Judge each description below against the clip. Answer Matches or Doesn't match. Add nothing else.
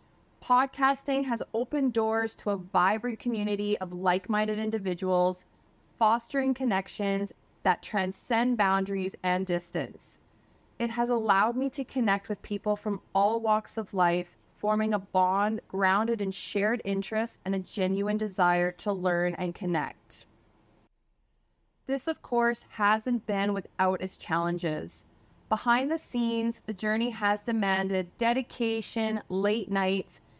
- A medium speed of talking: Doesn't match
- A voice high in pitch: Matches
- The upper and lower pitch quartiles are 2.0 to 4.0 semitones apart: Matches